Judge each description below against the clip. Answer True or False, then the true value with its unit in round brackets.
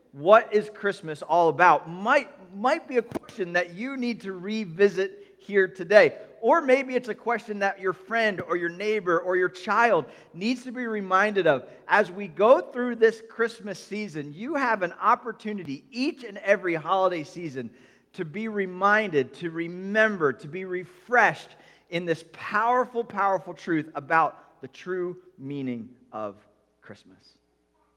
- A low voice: False (195 Hz)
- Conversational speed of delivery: True (150 wpm)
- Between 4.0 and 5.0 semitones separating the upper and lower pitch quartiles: True (4.5 semitones)